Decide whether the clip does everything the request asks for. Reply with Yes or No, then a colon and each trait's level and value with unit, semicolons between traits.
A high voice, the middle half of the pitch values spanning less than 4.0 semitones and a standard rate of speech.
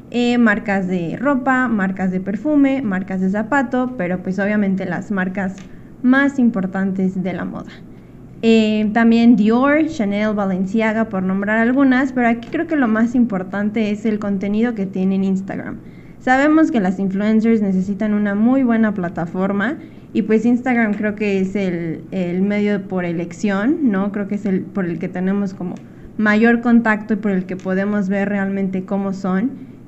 Yes: high, 205 Hz; average, 3.4 semitones; average, 165 wpm